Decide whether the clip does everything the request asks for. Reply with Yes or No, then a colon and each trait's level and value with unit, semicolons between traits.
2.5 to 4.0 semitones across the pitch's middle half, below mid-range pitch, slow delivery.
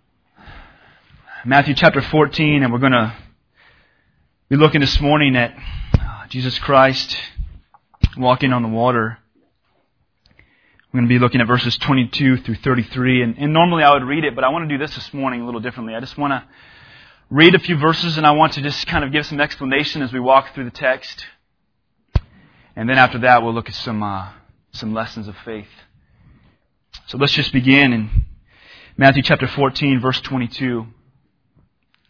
No: average, 3.4 semitones; low, 130 Hz; average, 175 wpm